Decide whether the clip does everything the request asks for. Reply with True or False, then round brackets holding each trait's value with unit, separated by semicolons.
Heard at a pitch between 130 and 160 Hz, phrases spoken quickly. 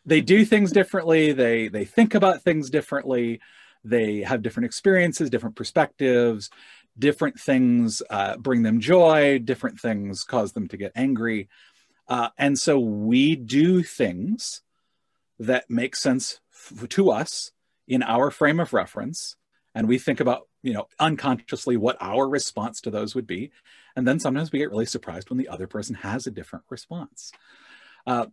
False (135 Hz; 160 wpm)